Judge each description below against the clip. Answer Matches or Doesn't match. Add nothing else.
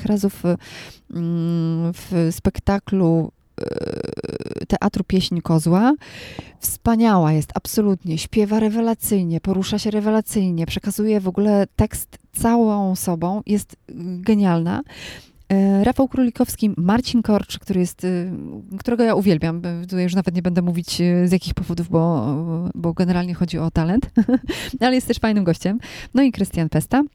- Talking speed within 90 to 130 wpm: Matches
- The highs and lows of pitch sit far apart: Doesn't match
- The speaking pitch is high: Matches